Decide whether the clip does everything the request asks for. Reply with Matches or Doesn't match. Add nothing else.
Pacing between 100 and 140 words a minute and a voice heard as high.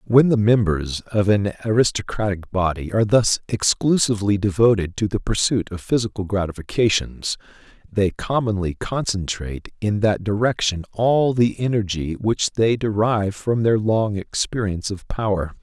Doesn't match